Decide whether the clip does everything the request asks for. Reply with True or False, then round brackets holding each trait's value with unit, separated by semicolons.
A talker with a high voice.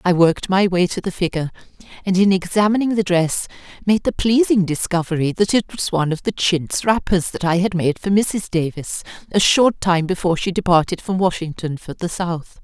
False (180 Hz)